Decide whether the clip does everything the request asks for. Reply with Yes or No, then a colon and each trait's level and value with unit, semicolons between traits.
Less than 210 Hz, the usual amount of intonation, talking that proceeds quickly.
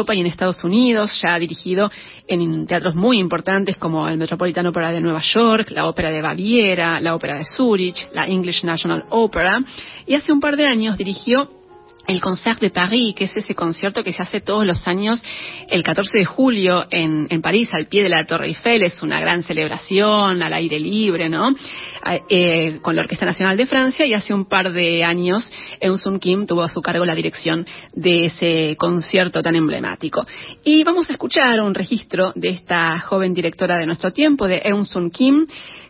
Yes: medium, 185 Hz; average, 4.1 semitones; fast, 195 wpm